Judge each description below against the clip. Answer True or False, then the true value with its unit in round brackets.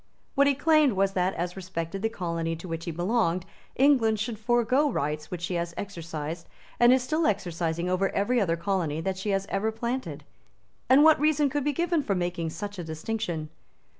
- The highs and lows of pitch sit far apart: True (6.4 semitones)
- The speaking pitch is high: True (195 Hz)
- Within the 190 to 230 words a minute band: True (195 wpm)